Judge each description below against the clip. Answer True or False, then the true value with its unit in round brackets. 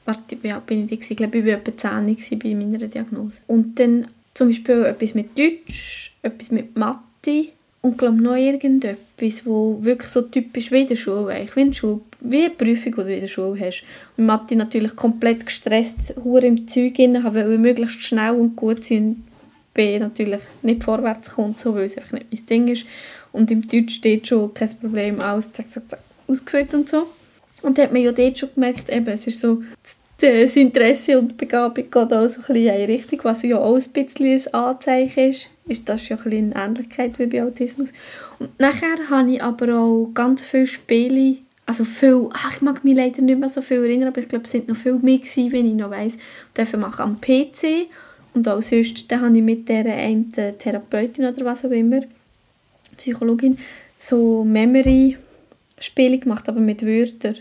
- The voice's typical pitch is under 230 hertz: False (240 Hz)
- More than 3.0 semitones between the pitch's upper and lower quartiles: False (2.7 semitones)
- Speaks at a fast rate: True (205 wpm)